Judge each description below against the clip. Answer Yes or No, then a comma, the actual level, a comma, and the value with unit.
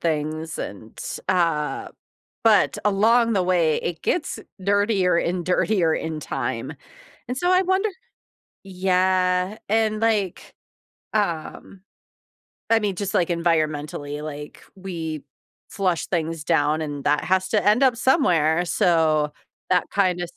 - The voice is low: No, medium, 180 Hz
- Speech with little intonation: No, average, 4.2 semitones